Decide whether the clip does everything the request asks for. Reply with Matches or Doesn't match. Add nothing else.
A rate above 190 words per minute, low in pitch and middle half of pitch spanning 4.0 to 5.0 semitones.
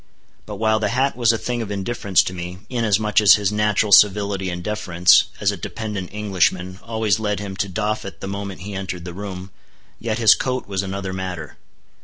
Doesn't match